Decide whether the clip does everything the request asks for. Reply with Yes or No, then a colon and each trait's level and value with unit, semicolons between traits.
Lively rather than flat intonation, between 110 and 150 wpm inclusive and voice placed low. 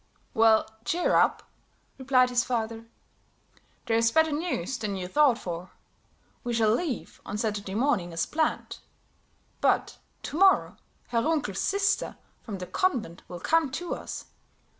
No: wide, 6.4 semitones; average, 140 wpm; high, 235 Hz